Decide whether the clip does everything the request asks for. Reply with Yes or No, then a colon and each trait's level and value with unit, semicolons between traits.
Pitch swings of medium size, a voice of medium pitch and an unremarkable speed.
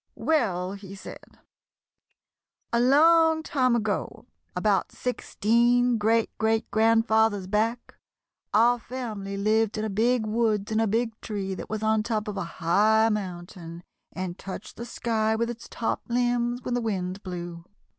No: average, 3.1 semitones; high, 220 Hz; average, 145 wpm